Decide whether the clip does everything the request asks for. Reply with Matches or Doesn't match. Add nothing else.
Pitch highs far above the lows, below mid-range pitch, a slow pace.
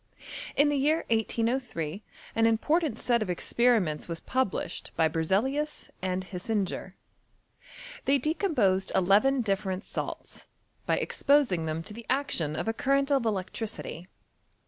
Doesn't match